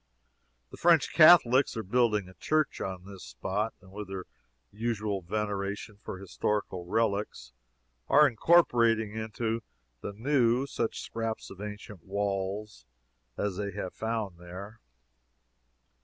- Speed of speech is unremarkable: No, slow, 125 wpm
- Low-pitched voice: Yes, low, 105 Hz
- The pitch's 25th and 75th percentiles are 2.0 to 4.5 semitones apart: Yes, average, 2.8 semitones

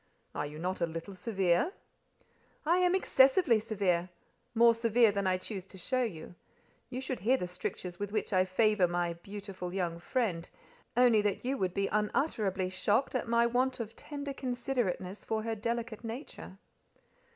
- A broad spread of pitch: No, average, 4.8 semitones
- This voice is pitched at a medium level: No, high, 210 Hz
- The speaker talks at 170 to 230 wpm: No, average, 160 wpm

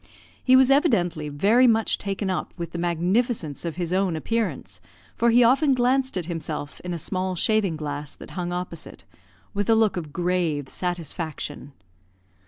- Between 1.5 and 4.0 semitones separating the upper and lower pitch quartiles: No, wide, 5.6 semitones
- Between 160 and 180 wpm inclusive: Yes, average, 165 wpm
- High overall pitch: No, medium, 180 Hz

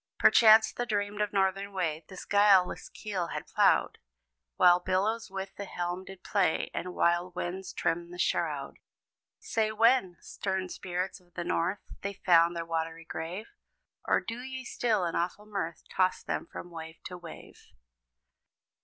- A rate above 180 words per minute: No, average, 155 wpm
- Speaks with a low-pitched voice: No, medium, 185 Hz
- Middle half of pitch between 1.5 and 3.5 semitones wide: Yes, average, 2.9 semitones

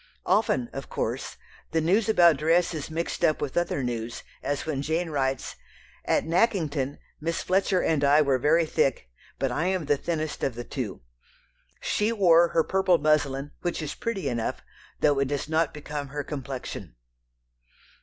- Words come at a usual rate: Yes, average, 165 wpm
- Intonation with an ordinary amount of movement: Yes, average, 3.7 semitones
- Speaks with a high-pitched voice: No, medium, 155 Hz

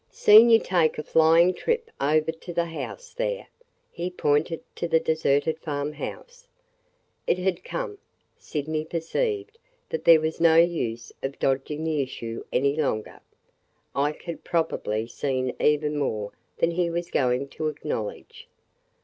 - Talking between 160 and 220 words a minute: No, average, 145 wpm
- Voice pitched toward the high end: No, medium, 160 Hz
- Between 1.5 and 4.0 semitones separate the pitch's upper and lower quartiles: Yes, average, 3.6 semitones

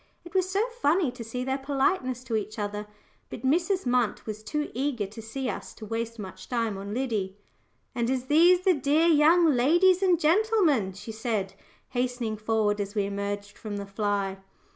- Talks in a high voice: Yes, high, 245 Hz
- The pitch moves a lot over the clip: Yes, wide, 6.2 semitones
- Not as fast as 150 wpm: No, average, 185 wpm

